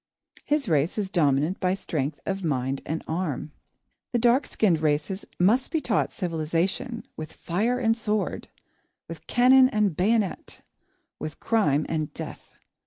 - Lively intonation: Yes, wide, 6.5 semitones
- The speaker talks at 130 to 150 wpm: Yes, average, 140 wpm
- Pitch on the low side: No, medium, 185 Hz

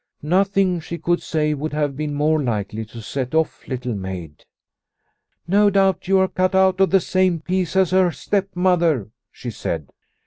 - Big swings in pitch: Yes, wide, 6.2 semitones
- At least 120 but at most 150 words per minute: No, average, 175 wpm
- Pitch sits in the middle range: Yes, medium, 165 Hz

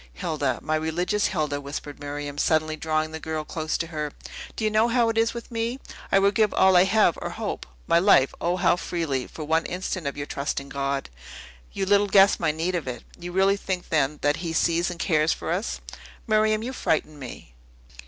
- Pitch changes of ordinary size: Yes, average, 4.5 semitones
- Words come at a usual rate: No, fast, 210 wpm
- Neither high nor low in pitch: Yes, medium, 165 Hz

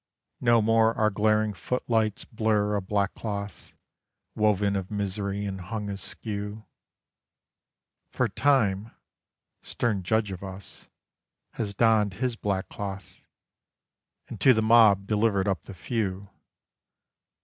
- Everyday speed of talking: No, slow, 115 wpm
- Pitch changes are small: Yes, narrow, 2.0 semitones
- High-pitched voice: No, low, 105 Hz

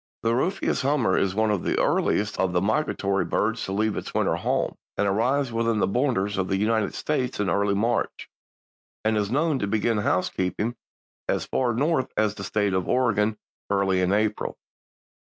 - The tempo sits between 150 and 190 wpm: Yes, average, 180 wpm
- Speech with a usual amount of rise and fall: Yes, average, 3.3 semitones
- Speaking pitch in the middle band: No, low, 105 Hz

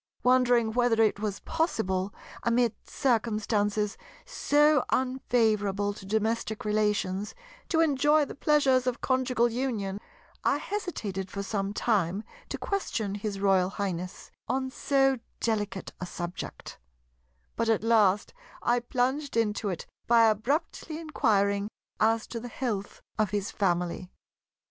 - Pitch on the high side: Yes, high, 220 Hz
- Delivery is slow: Yes, slow, 125 wpm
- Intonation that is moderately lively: Yes, average, 3.9 semitones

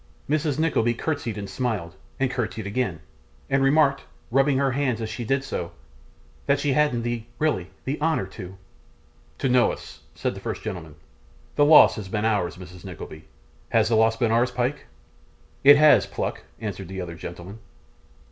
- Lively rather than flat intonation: Yes, wide, 5.9 semitones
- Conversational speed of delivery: Yes, average, 170 wpm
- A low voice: Yes, low, 115 Hz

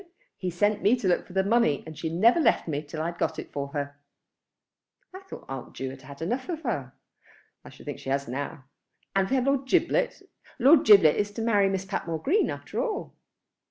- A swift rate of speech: Yes, fast, 220 wpm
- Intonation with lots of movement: Yes, wide, 8.5 semitones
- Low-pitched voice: No, high, 190 Hz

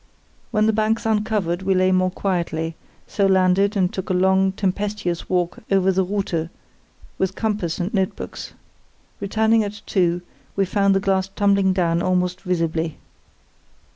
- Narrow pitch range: Yes, narrow, 2.0 semitones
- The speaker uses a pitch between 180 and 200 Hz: Yes, high, 190 Hz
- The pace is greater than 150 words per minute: No, average, 145 wpm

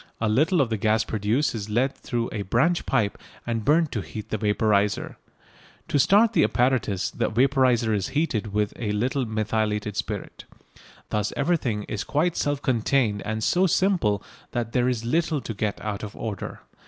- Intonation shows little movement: No, average, 4.5 semitones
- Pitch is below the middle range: Yes, low, 115 Hz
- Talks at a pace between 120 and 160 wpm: No, average, 175 wpm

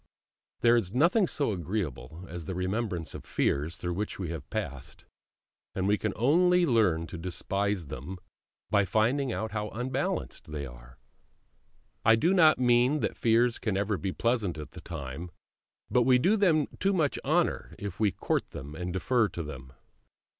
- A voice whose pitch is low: Yes, low, 105 Hz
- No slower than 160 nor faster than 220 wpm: Yes, average, 170 wpm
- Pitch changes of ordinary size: No, wide, 6.6 semitones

